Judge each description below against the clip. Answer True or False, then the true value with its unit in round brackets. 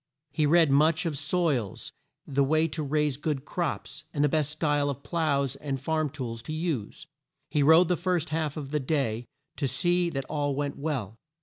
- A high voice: False (150 Hz)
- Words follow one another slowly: False (190 wpm)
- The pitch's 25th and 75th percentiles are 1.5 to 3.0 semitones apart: True (2.5 semitones)